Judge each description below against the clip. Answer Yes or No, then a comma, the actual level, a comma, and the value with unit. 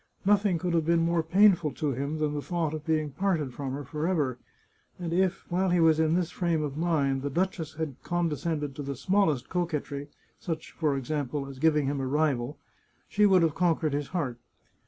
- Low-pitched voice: No, medium, 155 Hz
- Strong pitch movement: No, average, 3.3 semitones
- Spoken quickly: Yes, fast, 210 wpm